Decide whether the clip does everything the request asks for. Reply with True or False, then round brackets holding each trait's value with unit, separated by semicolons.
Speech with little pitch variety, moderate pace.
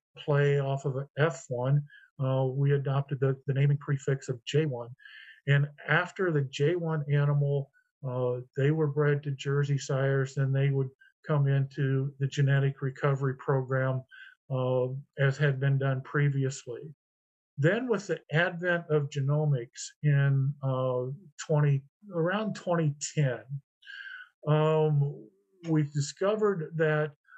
False (2.2 semitones; 125 wpm)